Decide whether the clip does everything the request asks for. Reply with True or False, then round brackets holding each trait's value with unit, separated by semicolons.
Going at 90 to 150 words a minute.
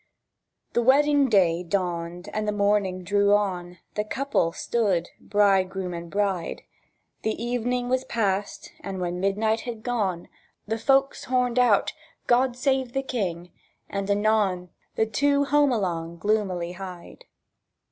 True (135 wpm)